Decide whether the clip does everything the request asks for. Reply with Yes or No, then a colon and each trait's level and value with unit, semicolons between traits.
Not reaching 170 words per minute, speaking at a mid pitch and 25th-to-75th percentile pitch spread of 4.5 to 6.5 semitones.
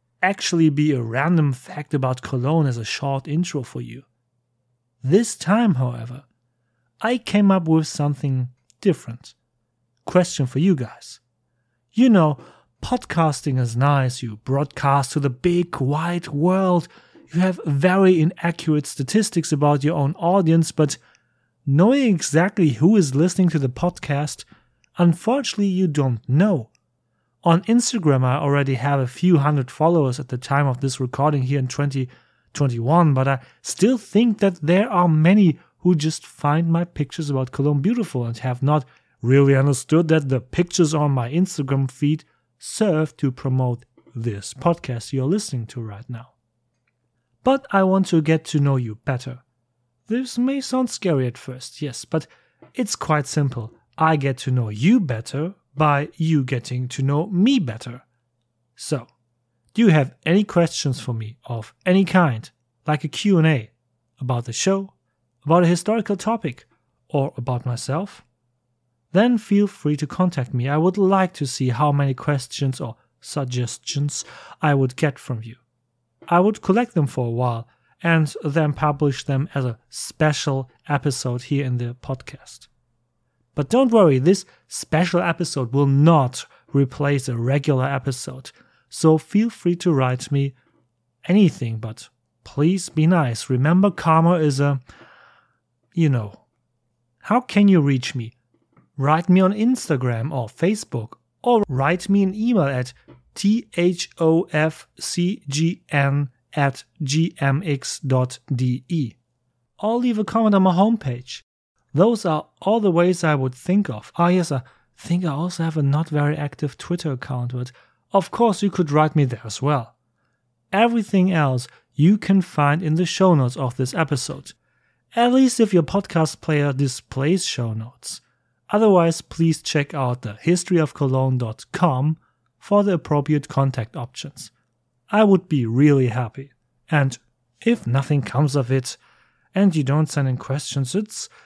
Yes: average, 150 wpm; medium, 145 Hz; wide, 5.5 semitones